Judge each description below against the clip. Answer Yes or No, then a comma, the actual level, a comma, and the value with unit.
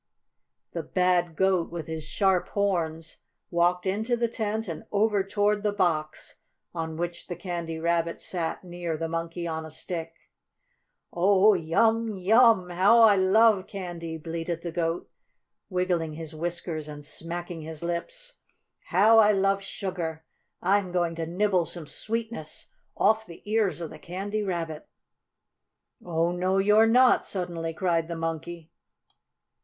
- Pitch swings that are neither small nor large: Yes, average, 3.4 semitones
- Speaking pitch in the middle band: Yes, medium, 175 Hz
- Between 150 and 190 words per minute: No, average, 140 wpm